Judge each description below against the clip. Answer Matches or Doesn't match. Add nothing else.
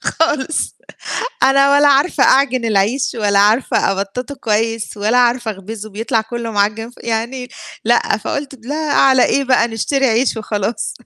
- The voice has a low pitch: Doesn't match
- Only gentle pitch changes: Doesn't match